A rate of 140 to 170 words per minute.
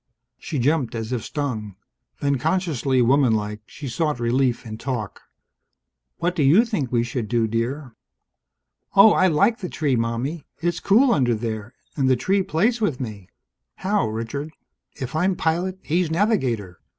Yes: average, 155 wpm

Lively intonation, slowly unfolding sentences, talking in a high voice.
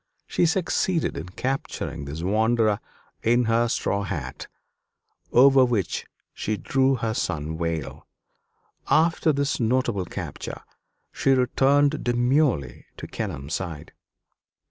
No: wide, 7.9 semitones; slow, 110 wpm; low, 115 Hz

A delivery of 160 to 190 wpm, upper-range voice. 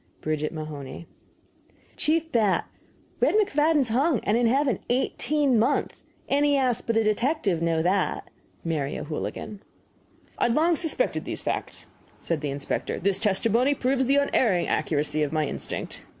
No: average, 150 wpm; high, 230 Hz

